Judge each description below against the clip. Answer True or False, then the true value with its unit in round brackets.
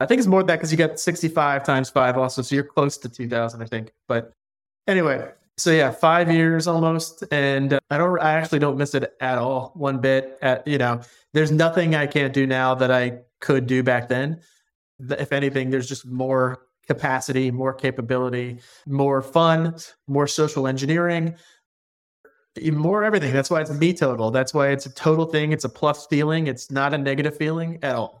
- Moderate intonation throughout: True (3.6 semitones)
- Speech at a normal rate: True (195 wpm)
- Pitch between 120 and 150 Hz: True (140 Hz)